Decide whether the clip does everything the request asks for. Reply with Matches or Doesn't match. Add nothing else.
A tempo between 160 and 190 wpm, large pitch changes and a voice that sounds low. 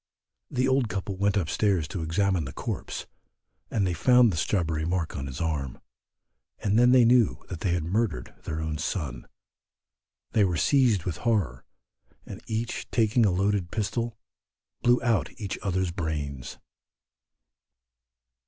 Doesn't match